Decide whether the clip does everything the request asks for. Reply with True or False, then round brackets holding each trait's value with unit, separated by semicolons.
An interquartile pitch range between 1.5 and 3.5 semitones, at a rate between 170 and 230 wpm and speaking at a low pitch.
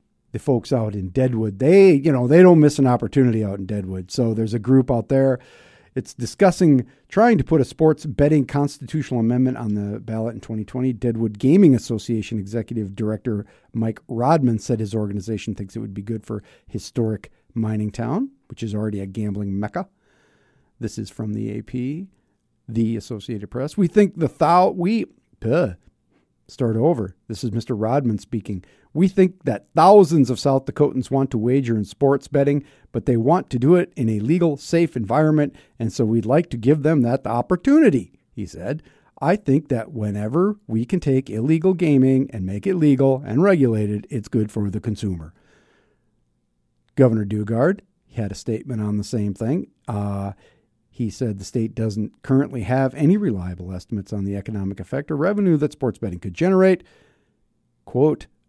False (5.0 semitones; 175 wpm; 120 Hz)